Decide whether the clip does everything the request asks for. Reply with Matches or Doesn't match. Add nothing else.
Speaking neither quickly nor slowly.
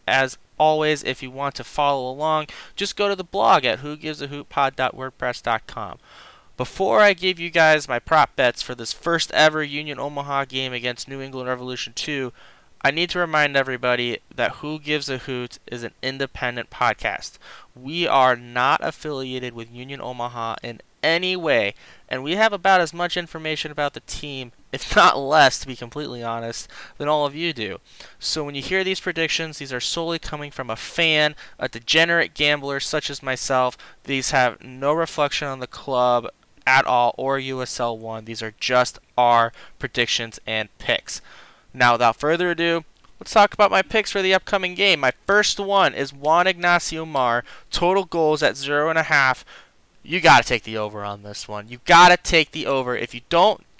Matches